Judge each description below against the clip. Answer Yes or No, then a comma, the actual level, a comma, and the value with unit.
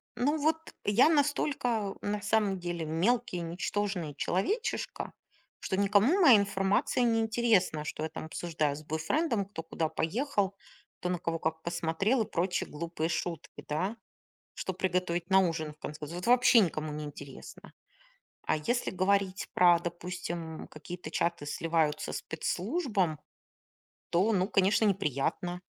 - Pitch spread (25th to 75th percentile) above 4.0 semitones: Yes, average, 4.5 semitones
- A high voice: No, medium, 180 Hz